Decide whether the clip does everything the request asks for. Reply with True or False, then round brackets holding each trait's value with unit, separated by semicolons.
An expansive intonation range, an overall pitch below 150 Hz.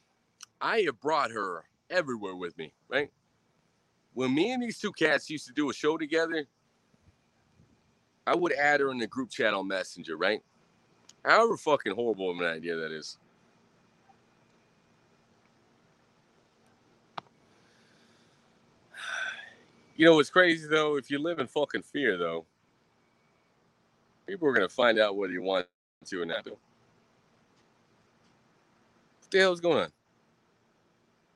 True (9.0 semitones; 140 Hz)